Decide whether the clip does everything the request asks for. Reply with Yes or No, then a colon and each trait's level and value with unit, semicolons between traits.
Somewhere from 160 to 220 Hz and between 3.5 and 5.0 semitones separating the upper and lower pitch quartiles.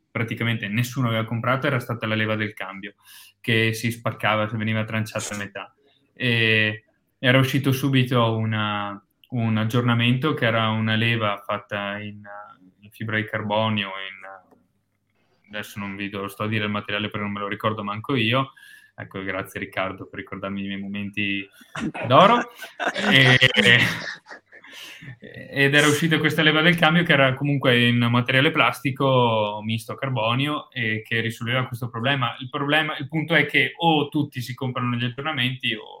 No: low, 115 Hz; average, 4.1 semitones